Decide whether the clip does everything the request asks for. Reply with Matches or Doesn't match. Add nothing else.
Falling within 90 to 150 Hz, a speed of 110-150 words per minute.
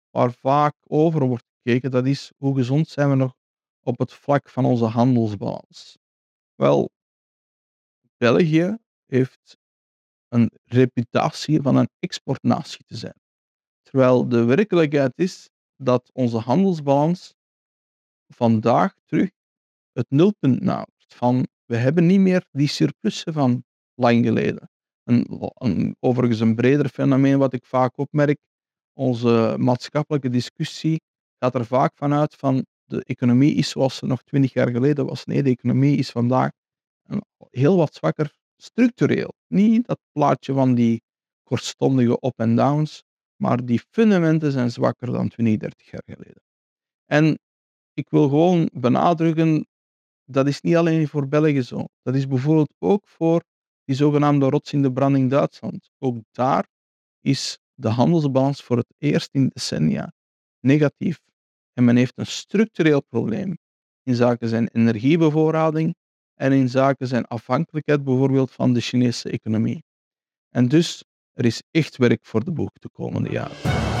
Matches